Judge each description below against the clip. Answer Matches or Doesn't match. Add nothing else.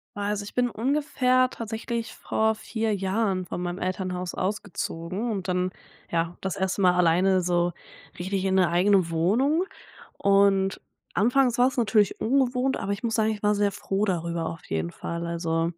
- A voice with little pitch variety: Doesn't match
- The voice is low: Doesn't match